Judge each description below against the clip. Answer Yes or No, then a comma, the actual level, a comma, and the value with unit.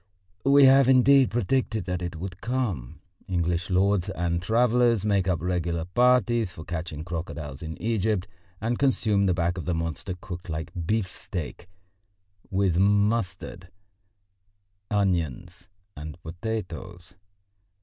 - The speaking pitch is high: No, very low, 90 Hz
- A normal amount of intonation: Yes, average, 4.5 semitones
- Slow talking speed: Yes, slow, 120 wpm